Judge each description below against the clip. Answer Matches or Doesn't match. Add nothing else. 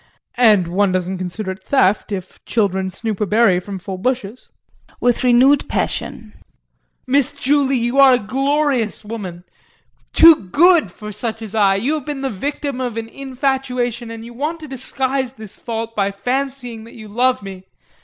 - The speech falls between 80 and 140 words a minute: Doesn't match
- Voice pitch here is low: Doesn't match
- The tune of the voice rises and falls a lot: Doesn't match